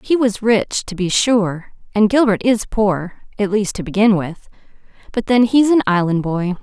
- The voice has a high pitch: Yes, high, 210 Hz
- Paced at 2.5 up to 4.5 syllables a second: Yes, 4.4 syllables/s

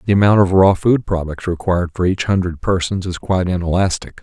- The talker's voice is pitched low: Yes, very low, 90 Hz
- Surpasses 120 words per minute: Yes, average, 200 wpm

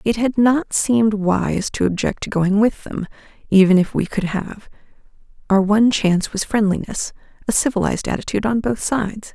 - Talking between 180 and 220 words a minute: No, average, 165 wpm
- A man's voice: No, female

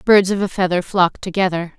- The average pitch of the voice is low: No, medium, 185 Hz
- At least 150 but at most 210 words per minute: Yes, average, 200 wpm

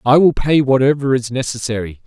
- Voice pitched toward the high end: No, low, 130 Hz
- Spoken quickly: No, average, 175 wpm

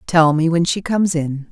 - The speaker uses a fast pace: Yes, fast, 240 wpm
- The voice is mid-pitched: Yes, medium, 165 Hz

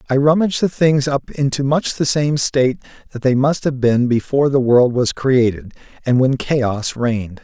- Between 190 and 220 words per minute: Yes, average, 195 wpm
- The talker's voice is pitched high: No, low, 130 Hz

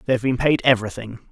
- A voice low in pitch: Yes, low, 120 Hz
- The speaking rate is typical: No, fast, 275 wpm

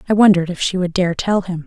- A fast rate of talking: Yes, fast, 290 wpm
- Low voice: No, medium, 185 Hz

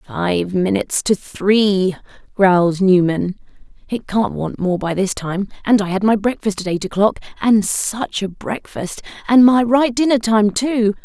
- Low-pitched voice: No, high, 205 Hz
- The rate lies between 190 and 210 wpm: No, average, 170 wpm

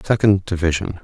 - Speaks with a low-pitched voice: Yes, very low, 95 Hz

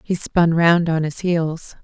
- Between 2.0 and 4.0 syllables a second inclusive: Yes, 3.6 syllables/s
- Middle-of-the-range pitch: Yes, medium, 165 Hz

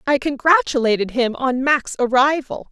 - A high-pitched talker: Yes, very high, 265 Hz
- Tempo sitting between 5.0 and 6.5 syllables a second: No, 4.7 syllables/s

